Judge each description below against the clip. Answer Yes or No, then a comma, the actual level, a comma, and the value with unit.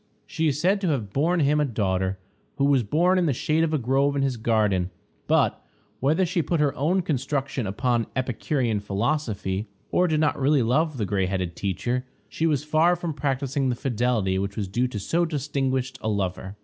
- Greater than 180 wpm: Yes, average, 200 wpm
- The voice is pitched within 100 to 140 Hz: Yes, low, 135 Hz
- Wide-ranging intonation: Yes, wide, 6.1 semitones